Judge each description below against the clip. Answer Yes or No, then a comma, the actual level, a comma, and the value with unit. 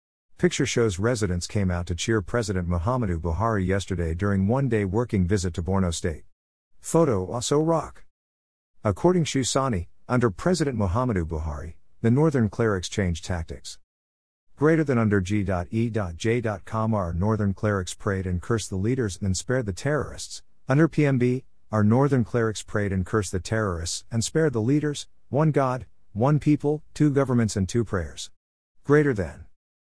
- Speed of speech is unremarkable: Yes, average, 150 wpm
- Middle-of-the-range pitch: No, low, 105 Hz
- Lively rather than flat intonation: Yes, wide, 5.7 semitones